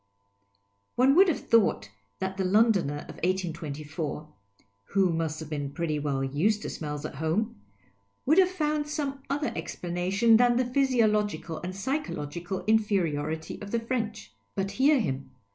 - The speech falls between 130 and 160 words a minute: Yes, average, 145 wpm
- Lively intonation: Yes, wide, 7.4 semitones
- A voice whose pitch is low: No, high, 190 Hz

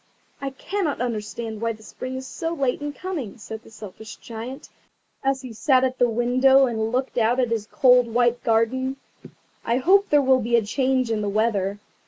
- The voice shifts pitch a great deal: No, average, 3.0 semitones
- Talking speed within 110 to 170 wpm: No, average, 195 wpm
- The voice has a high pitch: Yes, high, 245 Hz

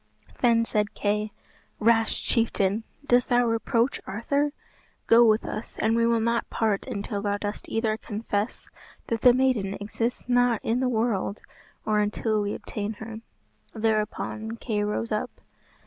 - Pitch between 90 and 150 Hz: No, high, 225 Hz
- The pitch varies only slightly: Yes, narrow, 1.8 semitones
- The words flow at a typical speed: Yes, average, 145 wpm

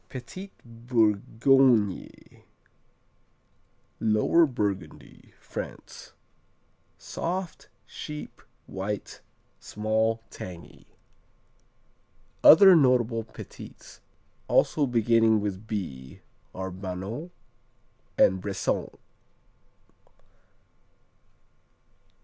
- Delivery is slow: Yes, slow, 55 wpm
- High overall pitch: No, low, 110 Hz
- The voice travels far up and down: No, average, 4.4 semitones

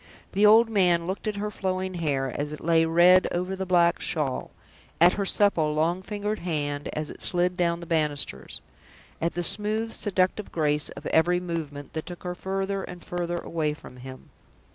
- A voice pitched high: No, medium, 175 Hz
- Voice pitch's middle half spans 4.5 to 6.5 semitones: No, average, 3.5 semitones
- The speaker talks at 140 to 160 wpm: No, average, 185 wpm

